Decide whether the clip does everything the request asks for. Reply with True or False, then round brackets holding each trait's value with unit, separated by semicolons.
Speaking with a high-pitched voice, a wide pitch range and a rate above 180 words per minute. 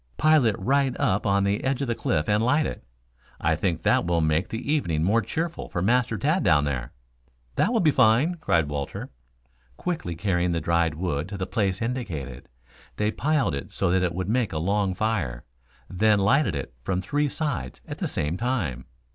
False (100 Hz; 7.4 semitones; 195 wpm)